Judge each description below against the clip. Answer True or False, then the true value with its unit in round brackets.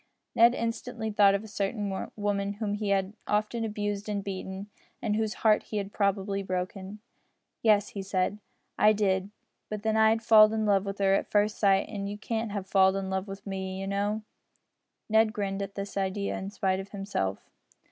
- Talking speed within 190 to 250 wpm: True (195 wpm)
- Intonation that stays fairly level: True (1.6 semitones)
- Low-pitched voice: False (200 Hz)